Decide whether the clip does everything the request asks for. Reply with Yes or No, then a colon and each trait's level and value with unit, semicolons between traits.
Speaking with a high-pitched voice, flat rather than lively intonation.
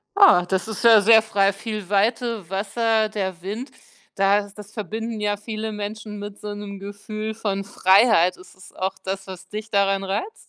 Yes: high, 205 Hz; narrow, 1.9 semitones